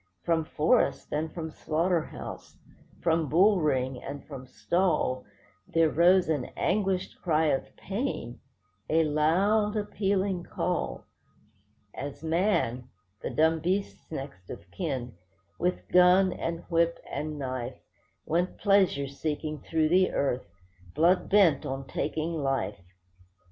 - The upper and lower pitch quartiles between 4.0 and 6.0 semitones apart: Yes, average, 5.0 semitones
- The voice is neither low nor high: Yes, medium, 160 Hz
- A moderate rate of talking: No, slow, 115 wpm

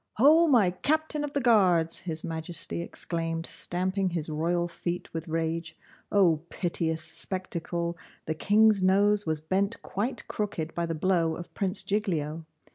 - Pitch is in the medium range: Yes, medium, 175 Hz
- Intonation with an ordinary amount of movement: Yes, average, 3.6 semitones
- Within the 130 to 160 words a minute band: Yes, average, 145 wpm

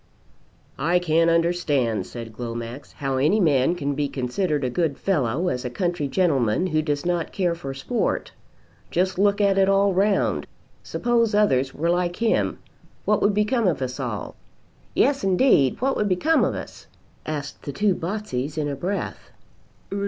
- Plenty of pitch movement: Yes, wide, 6.2 semitones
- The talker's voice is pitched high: No, medium, 170 Hz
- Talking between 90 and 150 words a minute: No, average, 165 wpm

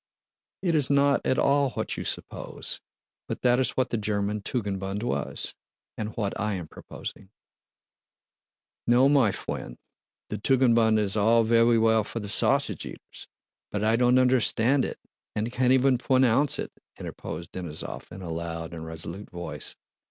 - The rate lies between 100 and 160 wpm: Yes, average, 155 wpm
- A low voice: Yes, low, 110 Hz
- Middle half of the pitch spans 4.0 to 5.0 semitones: Yes, average, 4.4 semitones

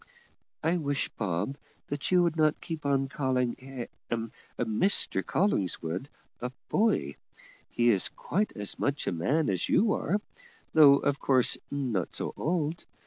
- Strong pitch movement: Yes, wide, 6.0 semitones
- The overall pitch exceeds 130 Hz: Yes, medium, 140 Hz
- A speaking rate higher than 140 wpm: No, slow, 135 wpm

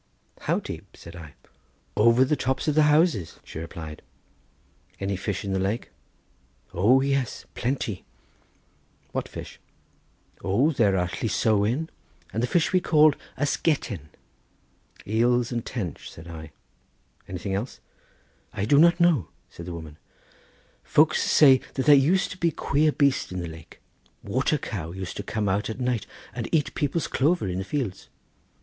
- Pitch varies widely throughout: Yes, wide, 7.4 semitones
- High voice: No, low, 115 Hz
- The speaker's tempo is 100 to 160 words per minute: Yes, average, 155 wpm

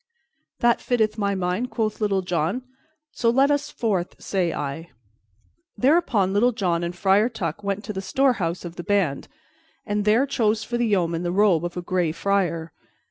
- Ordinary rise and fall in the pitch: Yes, average, 4.5 semitones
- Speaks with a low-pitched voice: No, high, 200 Hz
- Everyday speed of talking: Yes, average, 175 wpm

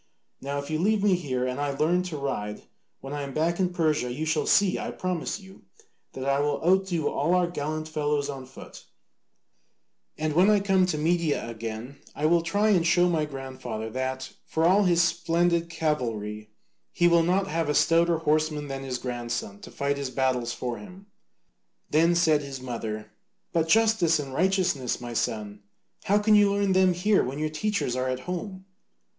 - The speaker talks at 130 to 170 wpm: No, average, 185 wpm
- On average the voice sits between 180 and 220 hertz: No, medium, 155 Hz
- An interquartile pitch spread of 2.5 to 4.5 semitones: No, average, 5.1 semitones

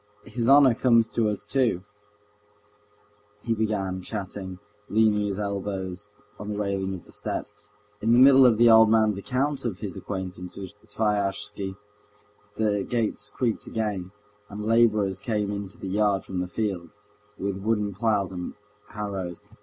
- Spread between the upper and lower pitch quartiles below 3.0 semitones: Yes, narrow, 2.6 semitones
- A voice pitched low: Yes, low, 105 Hz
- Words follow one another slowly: No, average, 150 wpm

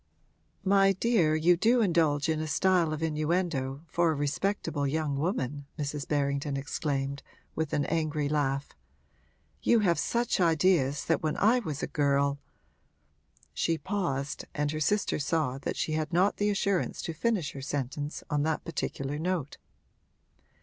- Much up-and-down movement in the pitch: No, average, 3.6 semitones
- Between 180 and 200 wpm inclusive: No, average, 150 wpm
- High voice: No, medium, 155 Hz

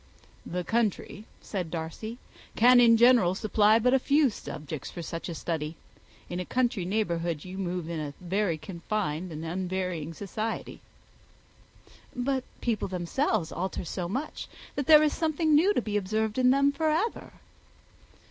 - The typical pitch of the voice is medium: No, high, 200 Hz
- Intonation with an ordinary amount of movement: No, wide, 6.4 semitones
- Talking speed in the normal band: Yes, average, 150 wpm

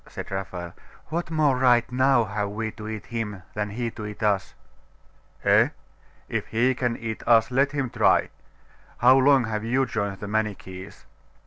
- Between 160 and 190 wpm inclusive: Yes, average, 170 wpm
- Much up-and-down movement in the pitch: No, average, 3.6 semitones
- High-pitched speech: No, low, 115 Hz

